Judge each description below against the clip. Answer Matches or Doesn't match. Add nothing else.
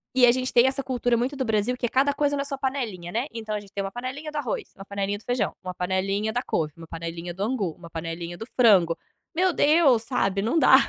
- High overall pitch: Matches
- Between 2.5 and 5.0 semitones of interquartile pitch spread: Doesn't match